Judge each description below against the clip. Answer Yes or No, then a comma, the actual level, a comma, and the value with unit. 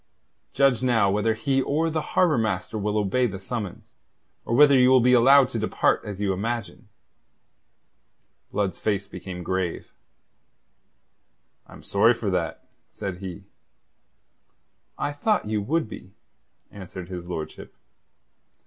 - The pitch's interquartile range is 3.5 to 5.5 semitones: Yes, average, 5.1 semitones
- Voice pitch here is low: Yes, low, 110 Hz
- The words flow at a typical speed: No, slow, 130 wpm